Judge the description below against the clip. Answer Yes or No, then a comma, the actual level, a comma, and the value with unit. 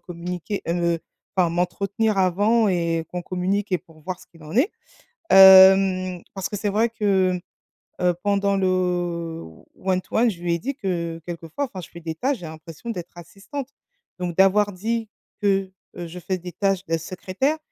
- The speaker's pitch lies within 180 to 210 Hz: Yes, medium, 185 Hz